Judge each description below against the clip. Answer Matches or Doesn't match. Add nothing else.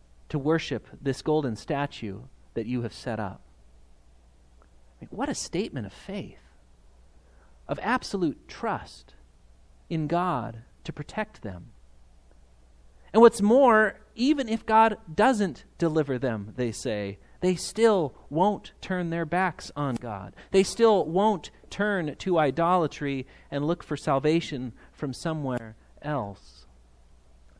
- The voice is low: Matches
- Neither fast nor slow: Doesn't match